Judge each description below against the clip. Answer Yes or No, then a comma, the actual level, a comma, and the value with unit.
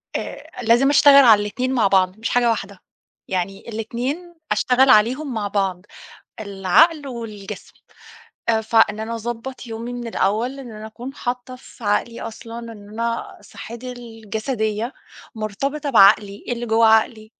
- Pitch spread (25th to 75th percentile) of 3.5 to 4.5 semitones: No, average, 2.8 semitones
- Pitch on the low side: No, high, 230 Hz